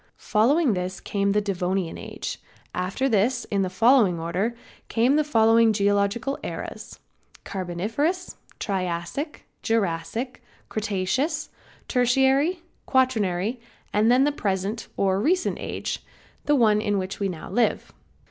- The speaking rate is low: Yes, slow, 120 wpm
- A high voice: Yes, high, 215 Hz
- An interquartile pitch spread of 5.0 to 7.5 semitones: Yes, average, 5.3 semitones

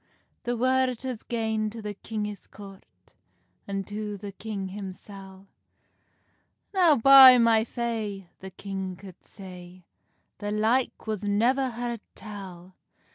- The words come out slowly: Yes, slow, 125 wpm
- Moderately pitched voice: No, high, 210 Hz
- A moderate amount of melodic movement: Yes, average, 3.3 semitones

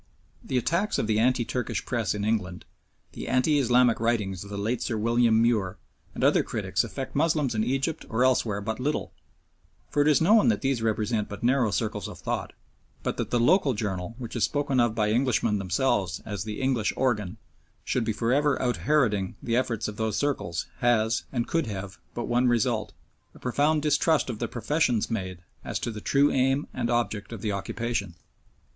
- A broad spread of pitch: No, average, 3.7 semitones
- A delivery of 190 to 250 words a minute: Yes, average, 195 wpm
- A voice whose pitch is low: Yes, low, 120 Hz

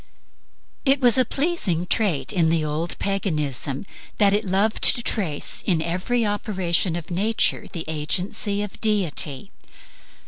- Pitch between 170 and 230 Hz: Yes, high, 190 Hz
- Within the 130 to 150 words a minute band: Yes, slow, 135 wpm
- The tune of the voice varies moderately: Yes, average, 4.6 semitones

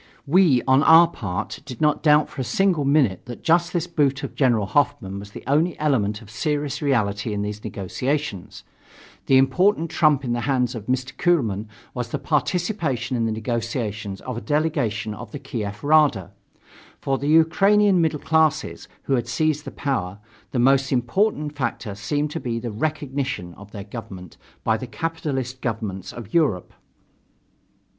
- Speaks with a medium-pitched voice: No, low, 130 Hz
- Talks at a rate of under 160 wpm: No, average, 165 wpm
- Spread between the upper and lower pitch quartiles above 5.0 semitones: Yes, wide, 5.5 semitones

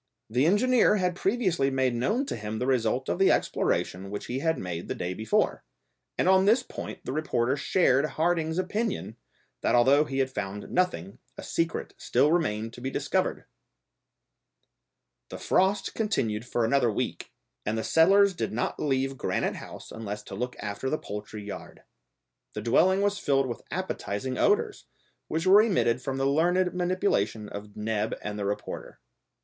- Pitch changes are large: Yes, wide, 8.7 semitones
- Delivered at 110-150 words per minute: No, average, 165 wpm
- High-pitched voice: No, low, 135 Hz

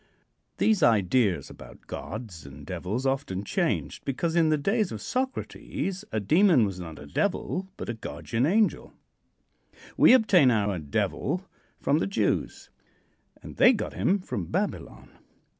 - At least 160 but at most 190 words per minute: No, average, 140 wpm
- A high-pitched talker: No, low, 130 Hz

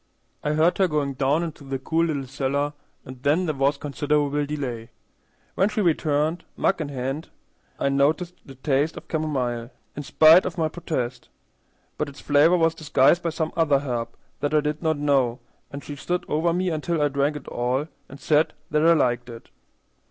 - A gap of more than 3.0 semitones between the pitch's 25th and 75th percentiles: No, average, 2.7 semitones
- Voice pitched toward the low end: No, medium, 145 Hz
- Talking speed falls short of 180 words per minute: No, average, 190 wpm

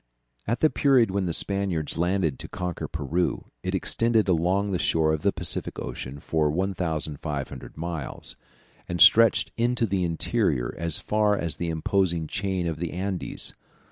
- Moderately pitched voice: No, very low, 85 Hz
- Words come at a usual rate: Yes, average, 155 wpm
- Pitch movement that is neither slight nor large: Yes, average, 3.7 semitones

